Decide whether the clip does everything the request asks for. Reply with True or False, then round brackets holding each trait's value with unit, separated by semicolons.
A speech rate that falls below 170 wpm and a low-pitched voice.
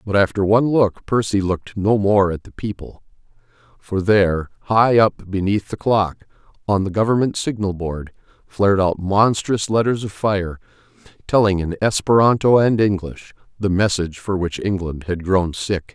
True (160 wpm; 100 Hz)